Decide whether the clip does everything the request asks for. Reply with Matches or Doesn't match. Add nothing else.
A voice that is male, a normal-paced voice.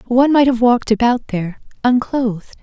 Doesn't match